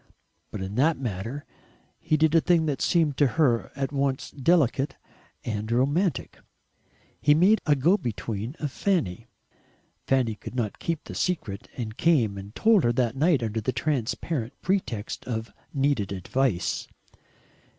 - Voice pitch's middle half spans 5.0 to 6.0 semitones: Yes, wide, 5.6 semitones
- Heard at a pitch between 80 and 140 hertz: Yes, low, 135 Hz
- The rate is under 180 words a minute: Yes, average, 150 wpm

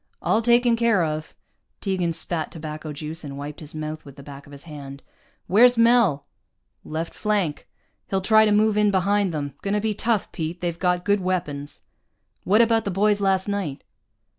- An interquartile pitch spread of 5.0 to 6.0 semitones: Yes, wide, 5.4 semitones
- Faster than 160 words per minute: Yes, average, 180 wpm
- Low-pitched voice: No, medium, 180 Hz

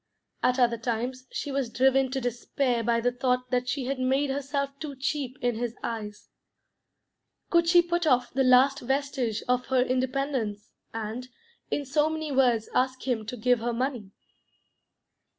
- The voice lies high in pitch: Yes, very high, 255 Hz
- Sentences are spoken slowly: No, average, 165 wpm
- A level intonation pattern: Yes, narrow, 2.3 semitones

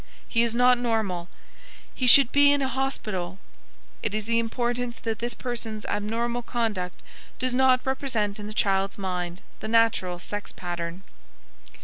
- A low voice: No, high, 225 Hz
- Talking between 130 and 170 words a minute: Yes, average, 145 wpm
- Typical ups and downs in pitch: Yes, average, 3.9 semitones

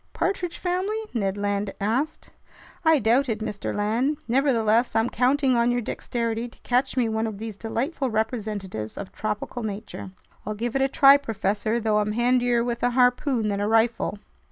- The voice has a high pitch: Yes, high, 230 Hz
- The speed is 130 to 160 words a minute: No, average, 175 wpm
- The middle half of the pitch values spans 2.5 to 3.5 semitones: Yes, average, 3.1 semitones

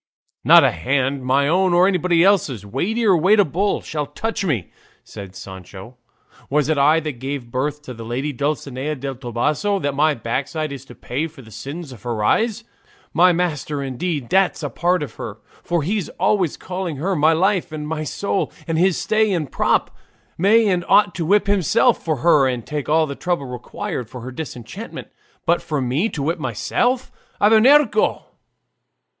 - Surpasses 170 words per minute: Yes, average, 180 wpm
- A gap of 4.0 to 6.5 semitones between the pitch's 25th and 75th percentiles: Yes, wide, 5.6 semitones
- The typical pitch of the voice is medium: Yes, medium, 155 Hz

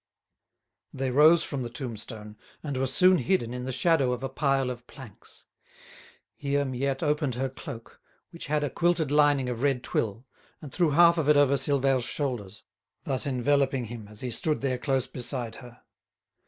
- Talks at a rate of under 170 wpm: No, average, 175 wpm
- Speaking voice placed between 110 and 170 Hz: Yes, low, 135 Hz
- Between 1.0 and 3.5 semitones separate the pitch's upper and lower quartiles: Yes, average, 2.8 semitones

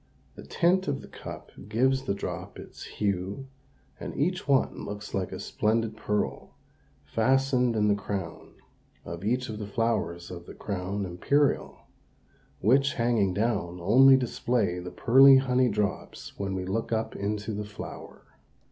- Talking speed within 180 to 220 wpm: No, average, 145 wpm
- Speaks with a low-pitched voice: Yes, low, 110 Hz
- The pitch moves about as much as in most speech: Yes, average, 4.5 semitones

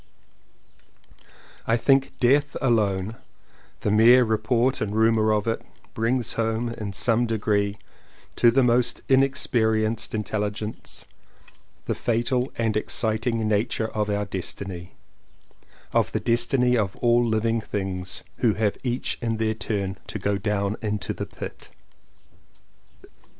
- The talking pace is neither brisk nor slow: No, slow, 130 wpm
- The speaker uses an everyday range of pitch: No, narrow, 2.2 semitones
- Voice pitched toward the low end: Yes, low, 110 Hz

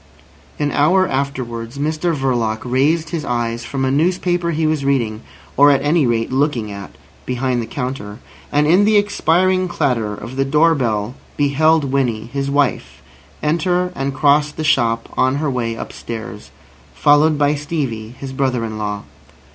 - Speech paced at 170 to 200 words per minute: No, average, 160 wpm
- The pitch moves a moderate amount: Yes, average, 4.7 semitones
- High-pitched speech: No, medium, 140 Hz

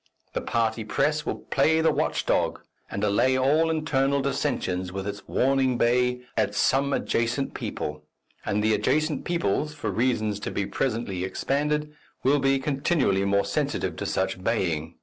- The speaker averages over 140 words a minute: Yes, average, 155 wpm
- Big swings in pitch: Yes, wide, 5.7 semitones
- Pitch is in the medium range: No, low, 125 Hz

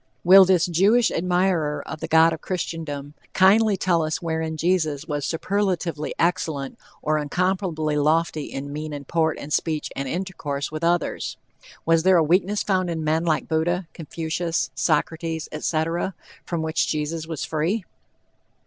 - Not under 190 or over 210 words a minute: No, average, 150 wpm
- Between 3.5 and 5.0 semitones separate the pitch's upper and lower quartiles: No, narrow, 2.6 semitones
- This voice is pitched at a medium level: Yes, medium, 165 Hz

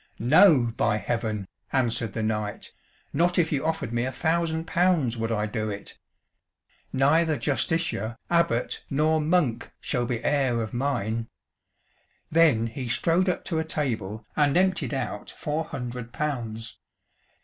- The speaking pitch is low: Yes, low, 130 Hz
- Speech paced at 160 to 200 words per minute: No, average, 140 wpm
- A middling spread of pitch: No, wide, 5.9 semitones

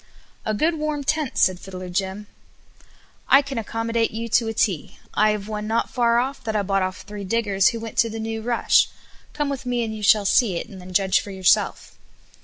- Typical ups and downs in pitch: Yes, average, 3.2 semitones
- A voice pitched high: Yes, high, 220 Hz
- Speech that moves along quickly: Yes, fast, 215 wpm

